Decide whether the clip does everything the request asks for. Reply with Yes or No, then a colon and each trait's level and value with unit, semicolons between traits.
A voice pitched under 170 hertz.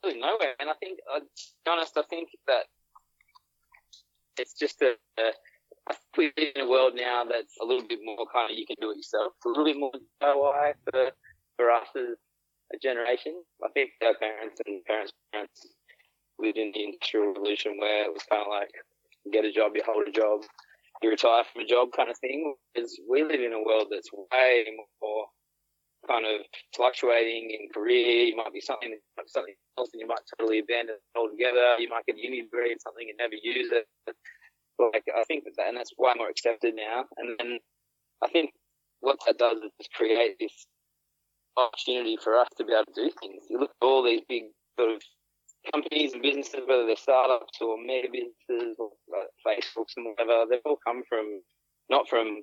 Yes: medium, 140 Hz